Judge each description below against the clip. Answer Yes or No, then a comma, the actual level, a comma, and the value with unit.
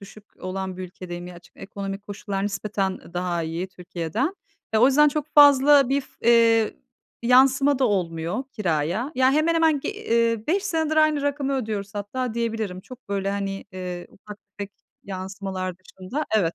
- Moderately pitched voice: No, high, 210 Hz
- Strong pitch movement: Yes, wide, 6.2 semitones